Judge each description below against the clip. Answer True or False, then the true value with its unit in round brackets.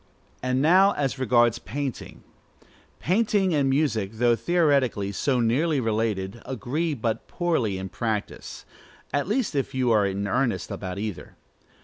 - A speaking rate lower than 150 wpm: True (135 wpm)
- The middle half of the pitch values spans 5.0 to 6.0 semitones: True (5.3 semitones)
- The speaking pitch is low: True (125 Hz)